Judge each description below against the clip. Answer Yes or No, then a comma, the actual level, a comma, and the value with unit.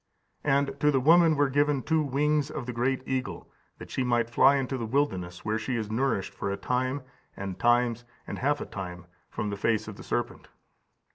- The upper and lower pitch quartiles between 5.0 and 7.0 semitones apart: No, average, 4.3 semitones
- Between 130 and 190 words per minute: No, fast, 205 wpm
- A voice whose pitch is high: No, low, 130 Hz